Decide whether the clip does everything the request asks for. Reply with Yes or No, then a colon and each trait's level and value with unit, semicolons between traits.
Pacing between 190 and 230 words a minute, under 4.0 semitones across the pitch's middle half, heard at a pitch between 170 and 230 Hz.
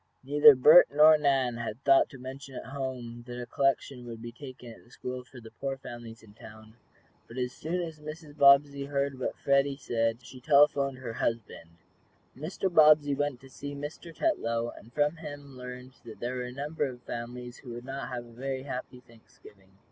No: average, 200 wpm; average, 3.0 semitones; low, 130 Hz